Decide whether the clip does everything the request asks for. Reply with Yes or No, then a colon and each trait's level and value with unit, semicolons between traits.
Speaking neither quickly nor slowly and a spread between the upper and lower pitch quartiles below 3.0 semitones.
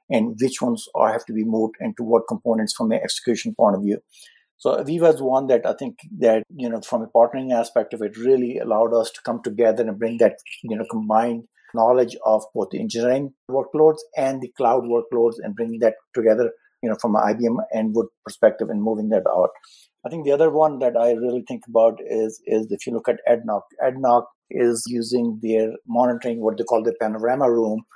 No: fast, 210 wpm; narrow, 2.5 semitones